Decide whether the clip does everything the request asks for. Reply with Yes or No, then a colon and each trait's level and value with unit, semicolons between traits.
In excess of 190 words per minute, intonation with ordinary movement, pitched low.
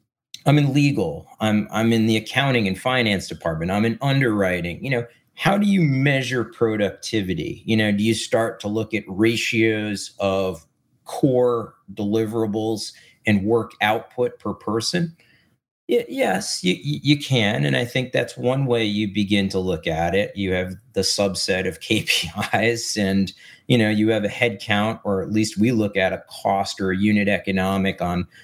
No: average, 170 wpm; average, 3.4 semitones; low, 110 Hz